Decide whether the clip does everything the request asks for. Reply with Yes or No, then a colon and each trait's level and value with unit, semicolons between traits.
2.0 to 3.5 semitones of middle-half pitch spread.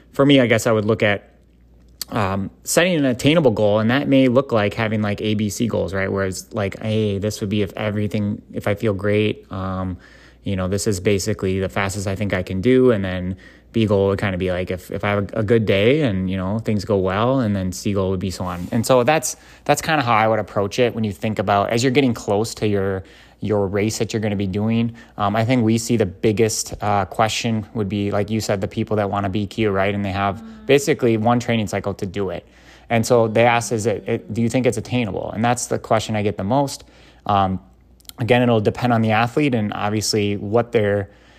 Yes: average, 2.8 semitones